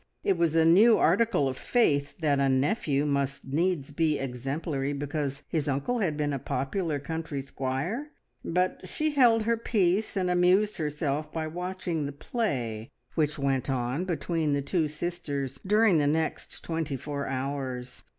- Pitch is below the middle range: No, medium, 150 Hz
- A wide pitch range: No, average, 4.4 semitones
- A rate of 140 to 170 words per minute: Yes, average, 160 wpm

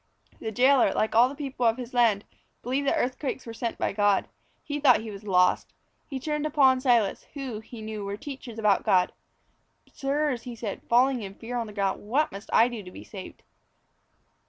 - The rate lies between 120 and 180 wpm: No, fast, 205 wpm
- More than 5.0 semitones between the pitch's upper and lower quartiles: No, average, 3.9 semitones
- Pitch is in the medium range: No, high, 235 Hz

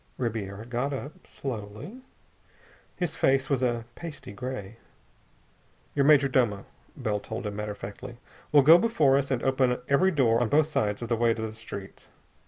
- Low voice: Yes, low, 125 Hz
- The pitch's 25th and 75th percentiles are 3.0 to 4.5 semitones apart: Yes, average, 4.2 semitones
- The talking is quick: No, average, 175 wpm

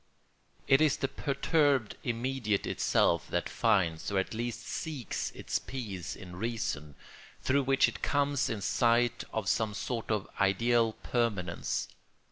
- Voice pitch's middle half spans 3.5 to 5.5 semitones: Yes, average, 5.0 semitones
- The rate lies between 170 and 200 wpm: No, slow, 135 wpm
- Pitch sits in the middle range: No, low, 115 Hz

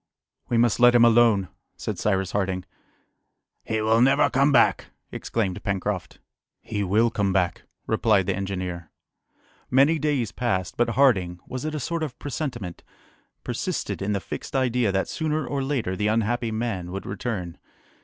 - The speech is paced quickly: No, average, 155 wpm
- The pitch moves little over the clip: No, average, 4.6 semitones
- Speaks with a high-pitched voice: No, low, 110 Hz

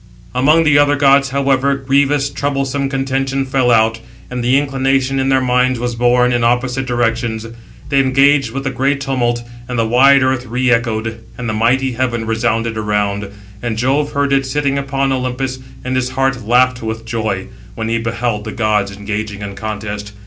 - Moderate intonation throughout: Yes, average, 3.0 semitones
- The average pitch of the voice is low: Yes, low, 125 Hz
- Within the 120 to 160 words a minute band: No, average, 180 wpm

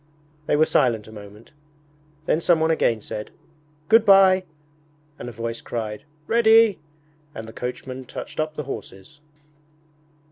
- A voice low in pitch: Yes, low, 130 Hz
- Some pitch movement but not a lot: No, wide, 7.4 semitones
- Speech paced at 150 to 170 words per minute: No, slow, 135 wpm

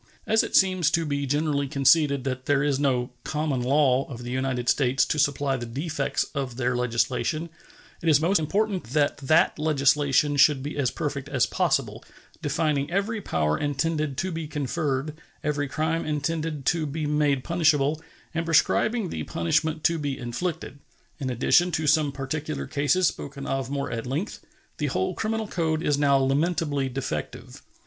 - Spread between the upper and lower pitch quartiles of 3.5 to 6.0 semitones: No, average, 2.9 semitones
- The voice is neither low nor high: Yes, medium, 145 Hz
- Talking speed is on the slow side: No, average, 165 wpm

